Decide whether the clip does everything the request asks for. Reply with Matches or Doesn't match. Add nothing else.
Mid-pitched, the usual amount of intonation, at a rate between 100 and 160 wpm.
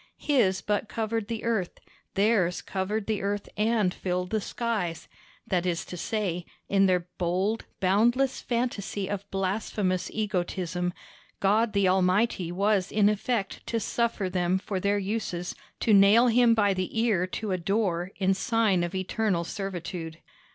Doesn't match